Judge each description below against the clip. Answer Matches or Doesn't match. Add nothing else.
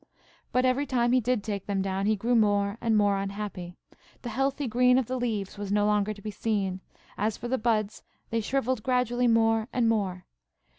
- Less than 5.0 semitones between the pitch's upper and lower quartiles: Matches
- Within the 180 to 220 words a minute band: Matches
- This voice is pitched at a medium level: Doesn't match